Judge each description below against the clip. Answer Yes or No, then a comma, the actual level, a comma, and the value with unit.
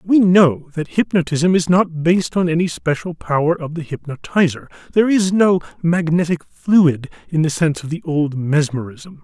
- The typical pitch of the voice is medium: Yes, medium, 165 Hz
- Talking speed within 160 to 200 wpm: Yes, average, 170 wpm